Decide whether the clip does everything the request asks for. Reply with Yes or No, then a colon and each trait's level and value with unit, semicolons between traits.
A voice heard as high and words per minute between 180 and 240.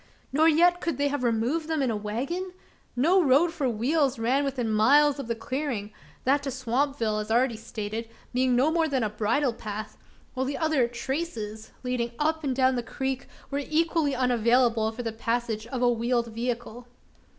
Yes: very high, 255 Hz; average, 185 wpm